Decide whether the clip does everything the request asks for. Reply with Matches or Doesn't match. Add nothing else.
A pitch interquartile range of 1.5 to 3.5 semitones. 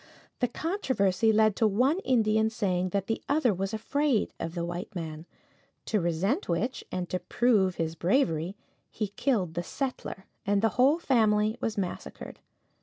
Doesn't match